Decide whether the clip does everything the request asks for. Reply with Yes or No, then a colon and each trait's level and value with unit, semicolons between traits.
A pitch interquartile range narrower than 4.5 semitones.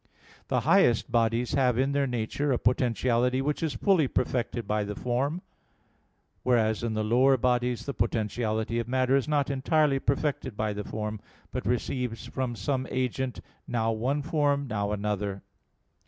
Yes: average, 3.4 semitones